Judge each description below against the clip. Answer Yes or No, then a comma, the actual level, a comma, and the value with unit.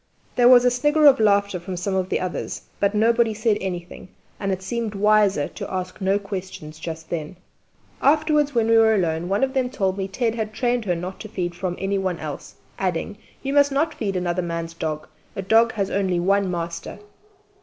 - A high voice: Yes, high, 195 Hz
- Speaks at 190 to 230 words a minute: Yes, fast, 205 wpm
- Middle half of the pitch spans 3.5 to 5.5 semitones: Yes, average, 4.2 semitones